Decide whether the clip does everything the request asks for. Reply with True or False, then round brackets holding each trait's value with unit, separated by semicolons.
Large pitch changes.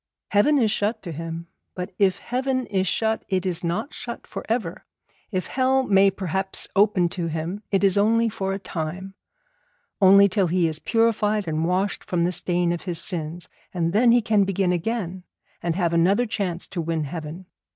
False (3.6 semitones)